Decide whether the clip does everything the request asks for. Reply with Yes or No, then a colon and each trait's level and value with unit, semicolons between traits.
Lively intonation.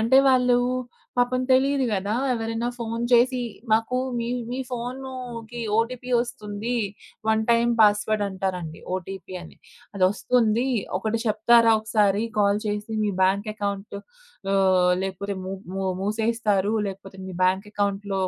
No: average, 3.3 semitones